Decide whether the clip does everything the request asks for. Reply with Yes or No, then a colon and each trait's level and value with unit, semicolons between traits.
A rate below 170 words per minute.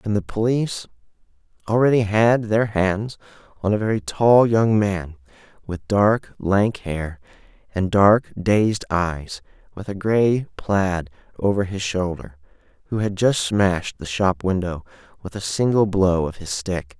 Yes: average, 150 wpm